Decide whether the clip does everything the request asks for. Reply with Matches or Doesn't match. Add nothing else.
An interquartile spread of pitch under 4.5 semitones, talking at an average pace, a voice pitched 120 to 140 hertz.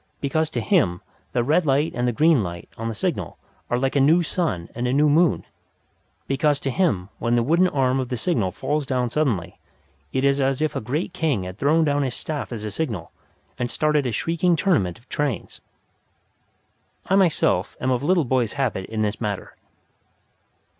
Doesn't match